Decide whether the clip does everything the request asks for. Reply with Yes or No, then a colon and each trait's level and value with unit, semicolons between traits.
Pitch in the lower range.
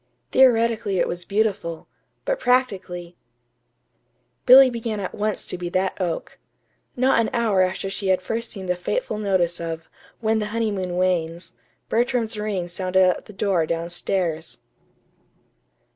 No: high, 195 Hz